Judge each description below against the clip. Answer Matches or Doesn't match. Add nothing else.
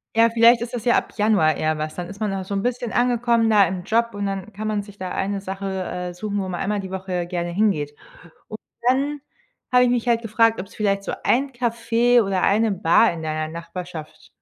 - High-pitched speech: Matches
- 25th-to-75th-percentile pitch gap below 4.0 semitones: Doesn't match